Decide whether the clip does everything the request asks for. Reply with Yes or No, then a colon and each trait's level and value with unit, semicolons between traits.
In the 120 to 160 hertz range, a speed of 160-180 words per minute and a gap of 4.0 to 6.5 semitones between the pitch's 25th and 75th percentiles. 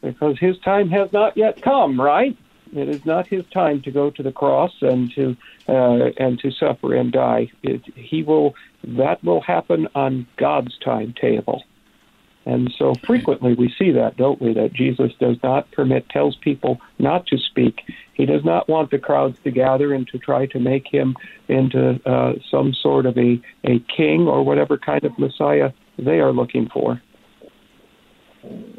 Yes: low, 135 Hz; average, 175 wpm; average, 4.9 semitones